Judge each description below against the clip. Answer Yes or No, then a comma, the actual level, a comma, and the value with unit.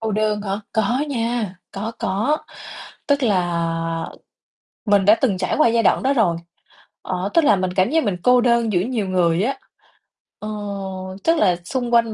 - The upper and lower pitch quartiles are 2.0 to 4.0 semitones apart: No, average, 4.4 semitones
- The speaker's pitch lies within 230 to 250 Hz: No, high, 215 Hz